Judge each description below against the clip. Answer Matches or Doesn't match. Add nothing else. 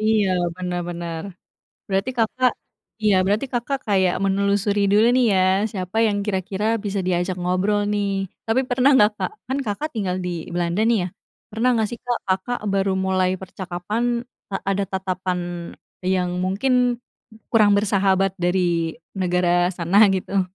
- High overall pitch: Matches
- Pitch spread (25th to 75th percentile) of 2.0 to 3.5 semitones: Matches